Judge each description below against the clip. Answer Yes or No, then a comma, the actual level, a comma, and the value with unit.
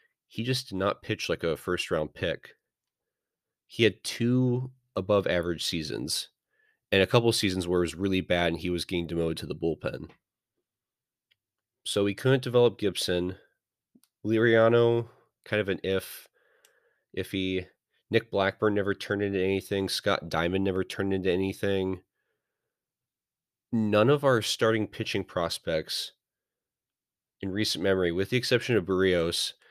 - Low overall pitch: Yes, very low, 95 Hz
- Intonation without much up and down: No, average, 3.3 semitones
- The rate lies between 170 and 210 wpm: No, average, 145 wpm